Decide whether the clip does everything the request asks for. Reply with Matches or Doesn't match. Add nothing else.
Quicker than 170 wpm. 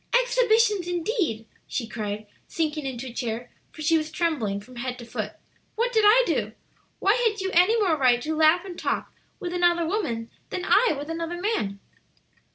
Matches